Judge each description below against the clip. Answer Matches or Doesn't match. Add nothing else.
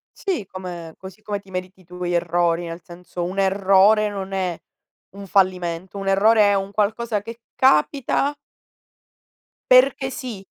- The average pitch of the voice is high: Matches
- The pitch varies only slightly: Doesn't match